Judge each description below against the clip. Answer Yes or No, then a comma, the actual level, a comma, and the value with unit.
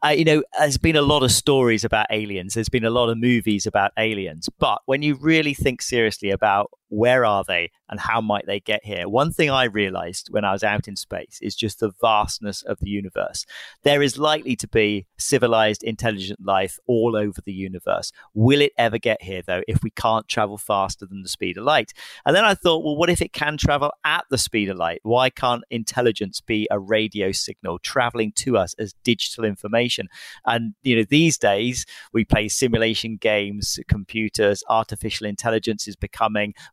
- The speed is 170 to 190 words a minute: No, average, 200 wpm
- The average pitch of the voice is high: No, low, 110 Hz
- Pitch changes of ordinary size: Yes, average, 3.8 semitones